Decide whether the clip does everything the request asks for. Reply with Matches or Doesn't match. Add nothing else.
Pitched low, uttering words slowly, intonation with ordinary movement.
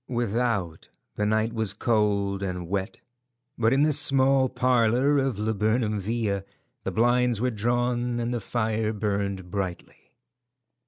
Matches